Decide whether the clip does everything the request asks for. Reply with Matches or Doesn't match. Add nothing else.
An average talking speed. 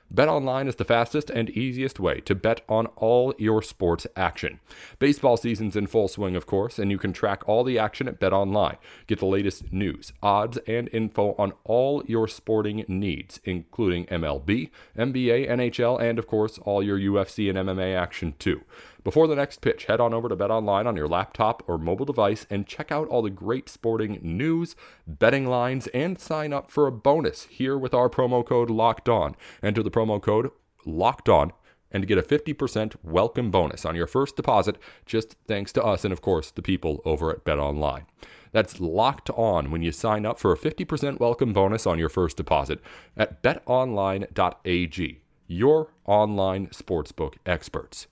Matches